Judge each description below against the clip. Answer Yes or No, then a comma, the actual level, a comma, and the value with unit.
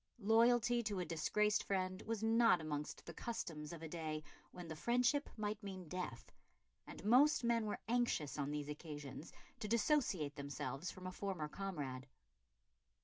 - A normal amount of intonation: No, wide, 6.9 semitones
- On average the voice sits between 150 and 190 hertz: Yes, medium, 185 Hz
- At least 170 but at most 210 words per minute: No, average, 155 wpm